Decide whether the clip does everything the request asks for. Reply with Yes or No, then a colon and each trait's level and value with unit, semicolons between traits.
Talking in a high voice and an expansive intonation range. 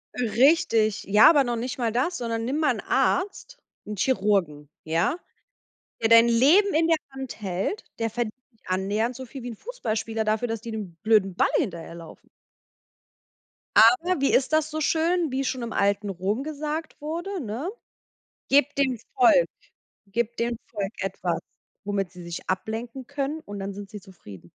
Yes: high, 230 Hz; wide, 5.8 semitones